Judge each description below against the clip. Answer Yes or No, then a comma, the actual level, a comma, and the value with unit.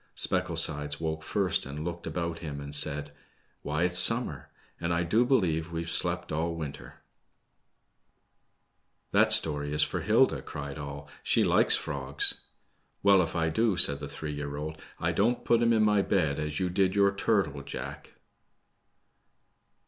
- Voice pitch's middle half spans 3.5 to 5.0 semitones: Yes, average, 4.4 semitones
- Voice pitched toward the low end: Yes, very low, 80 Hz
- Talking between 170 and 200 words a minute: No, average, 155 wpm